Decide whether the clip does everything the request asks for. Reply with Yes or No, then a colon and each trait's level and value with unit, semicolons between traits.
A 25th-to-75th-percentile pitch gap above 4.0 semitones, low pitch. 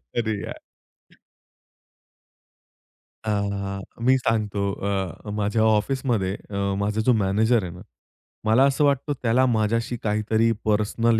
No: narrow, 2.4 semitones; low, 110 Hz